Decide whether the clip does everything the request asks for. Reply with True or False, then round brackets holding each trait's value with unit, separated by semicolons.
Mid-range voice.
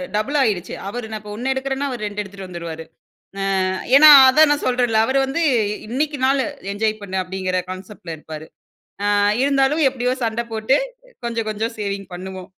False (220 Hz)